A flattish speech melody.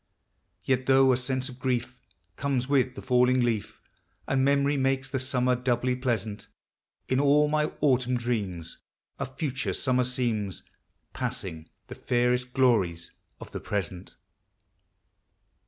Yes: narrow, 1.9 semitones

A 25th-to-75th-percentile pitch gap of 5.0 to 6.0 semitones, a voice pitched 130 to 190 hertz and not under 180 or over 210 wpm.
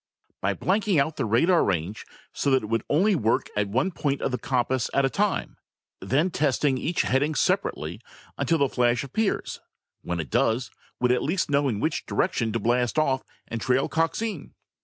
Yes: average, 5.3 semitones; low, 135 Hz; average, 185 wpm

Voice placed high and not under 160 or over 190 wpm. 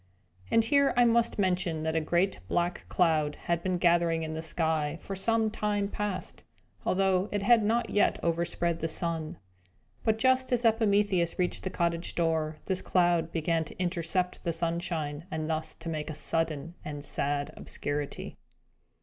No: medium, 170 Hz; average, 165 wpm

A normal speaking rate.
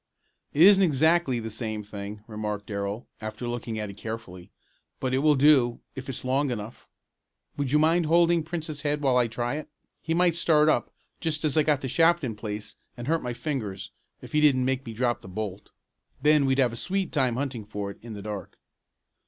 No: fast, 210 wpm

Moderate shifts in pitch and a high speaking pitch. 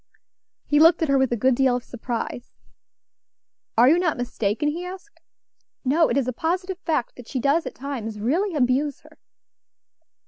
Yes: average, 4.9 semitones; very high, 275 Hz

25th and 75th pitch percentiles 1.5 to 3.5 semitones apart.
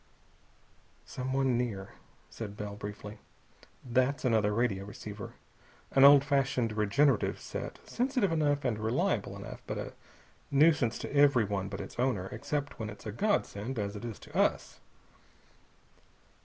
No: average, 4.9 semitones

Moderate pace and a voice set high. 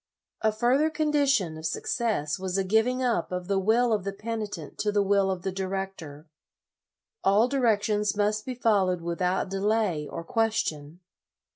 Yes: average, 155 wpm; high, 200 Hz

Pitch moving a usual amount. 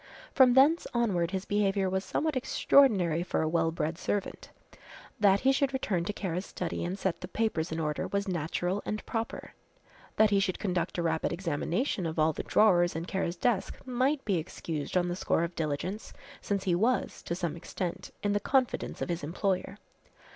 Yes: average, 3.9 semitones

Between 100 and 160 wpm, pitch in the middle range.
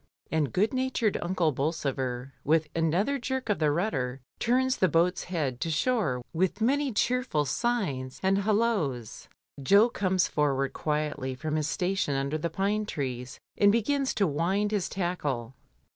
Yes: average, 150 wpm; medium, 170 Hz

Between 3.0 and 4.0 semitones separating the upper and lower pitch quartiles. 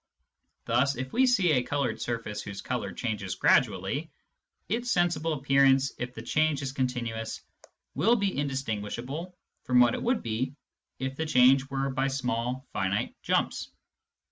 Yes: average, 3.6 semitones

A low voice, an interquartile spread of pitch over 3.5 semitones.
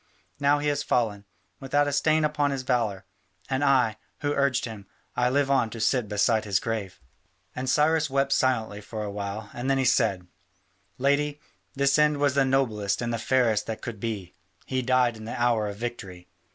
Yes: low, 125 Hz; average, 4.3 semitones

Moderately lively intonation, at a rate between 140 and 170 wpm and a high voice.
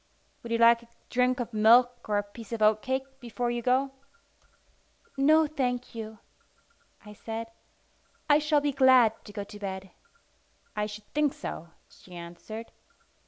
Yes: average, 3.5 semitones; average, 155 wpm; high, 235 Hz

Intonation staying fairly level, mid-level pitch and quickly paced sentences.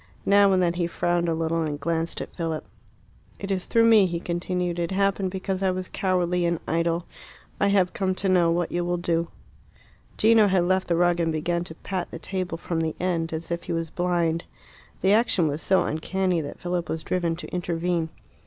Yes: narrow, 2.0 semitones; medium, 175 Hz; fast, 210 wpm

